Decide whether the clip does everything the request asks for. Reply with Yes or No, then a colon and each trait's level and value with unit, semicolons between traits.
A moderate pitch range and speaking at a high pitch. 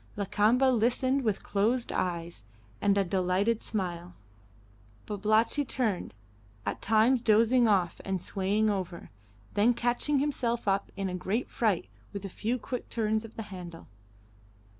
Yes: average, 3.7 semitones; high, 210 Hz